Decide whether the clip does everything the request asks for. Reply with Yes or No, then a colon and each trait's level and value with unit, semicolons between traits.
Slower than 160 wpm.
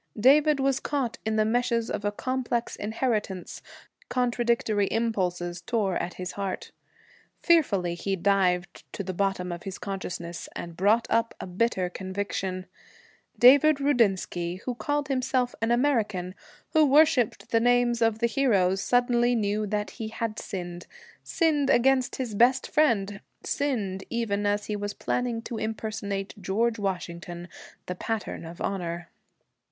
Yes: average, 140 wpm